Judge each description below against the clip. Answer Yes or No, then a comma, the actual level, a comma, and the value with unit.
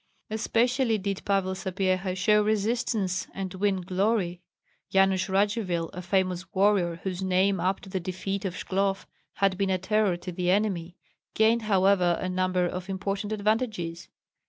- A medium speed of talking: Yes, average, 150 wpm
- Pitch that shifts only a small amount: Yes, narrow, 2.0 semitones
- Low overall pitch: No, high, 190 Hz